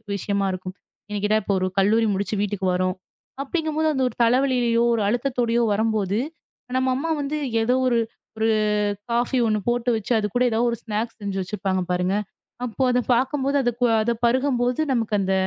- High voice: Yes, high, 230 Hz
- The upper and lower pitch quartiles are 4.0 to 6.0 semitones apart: No, average, 3.6 semitones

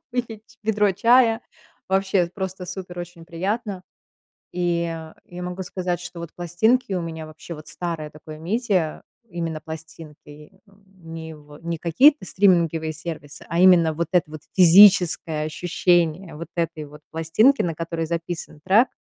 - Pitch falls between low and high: Yes, medium, 175 Hz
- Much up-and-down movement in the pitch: No, average, 2.9 semitones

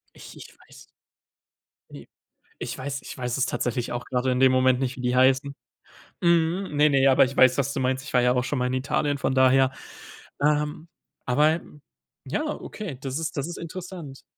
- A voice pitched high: No, low, 135 Hz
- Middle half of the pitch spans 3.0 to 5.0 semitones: No, narrow, 2.6 semitones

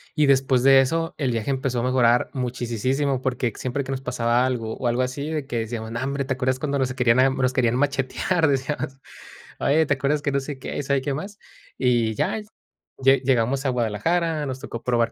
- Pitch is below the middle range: Yes, low, 130 Hz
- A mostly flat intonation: Yes, narrow, 2.2 semitones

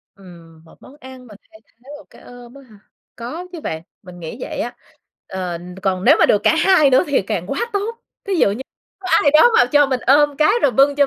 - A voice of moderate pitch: No, very high, 260 Hz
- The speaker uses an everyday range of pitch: No, wide, 6.9 semitones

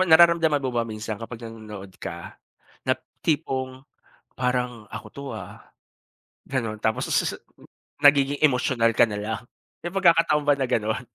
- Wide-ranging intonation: No, average, 4.5 semitones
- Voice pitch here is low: Yes, low, 125 Hz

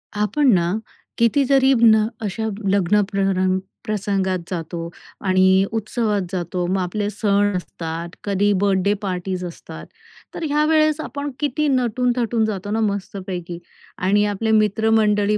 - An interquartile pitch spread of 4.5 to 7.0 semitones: No, average, 3.0 semitones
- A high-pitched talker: Yes, high, 205 Hz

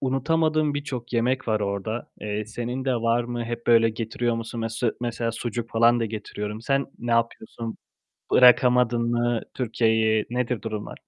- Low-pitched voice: Yes, low, 120 Hz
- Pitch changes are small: Yes, narrow, 1.6 semitones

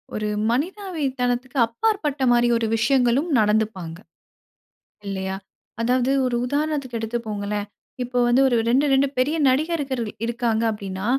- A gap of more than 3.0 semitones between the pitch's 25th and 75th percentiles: Yes, average, 4.1 semitones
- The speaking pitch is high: Yes, high, 245 Hz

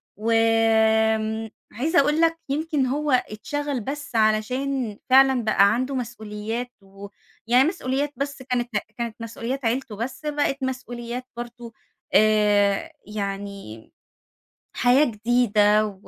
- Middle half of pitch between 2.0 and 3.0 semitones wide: No, average, 3.8 semitones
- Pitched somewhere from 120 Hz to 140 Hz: No, high, 235 Hz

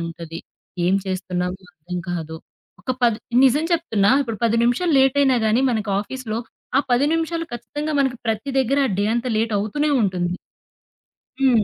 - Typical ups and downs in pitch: No, wide, 6.0 semitones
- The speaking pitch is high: Yes, high, 230 Hz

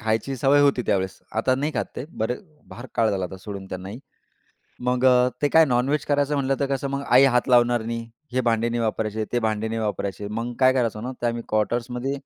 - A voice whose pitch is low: Yes, low, 120 Hz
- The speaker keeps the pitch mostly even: No, average, 3.1 semitones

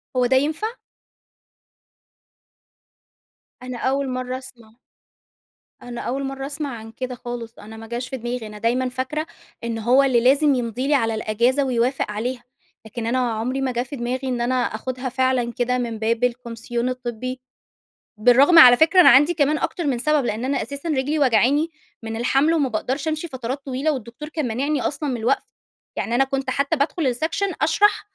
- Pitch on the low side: No, very high, 255 Hz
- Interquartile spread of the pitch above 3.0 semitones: No, average, 2.7 semitones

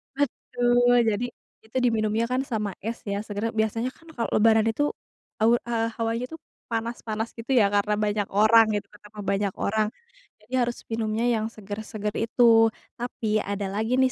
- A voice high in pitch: Yes, high, 220 Hz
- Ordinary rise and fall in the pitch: No, narrow, 1.9 semitones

